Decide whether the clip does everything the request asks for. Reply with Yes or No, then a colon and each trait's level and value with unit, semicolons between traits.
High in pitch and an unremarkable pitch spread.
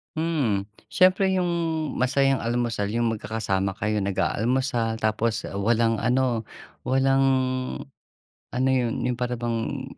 No: low, 120 Hz; average, 3.1 semitones